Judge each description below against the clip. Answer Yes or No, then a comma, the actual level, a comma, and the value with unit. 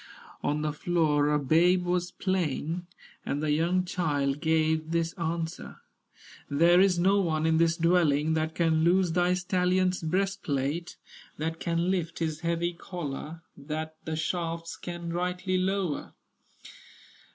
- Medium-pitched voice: Yes, medium, 165 Hz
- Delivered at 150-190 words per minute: No, slow, 135 wpm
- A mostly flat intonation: Yes, narrow, 2.2 semitones